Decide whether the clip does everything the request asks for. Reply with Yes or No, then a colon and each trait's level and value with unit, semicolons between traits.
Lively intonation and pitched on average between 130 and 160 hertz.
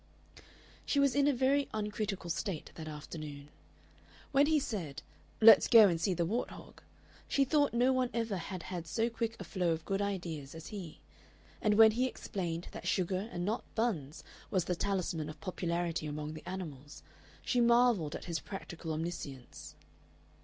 No: wide, 5.9 semitones; medium, 185 Hz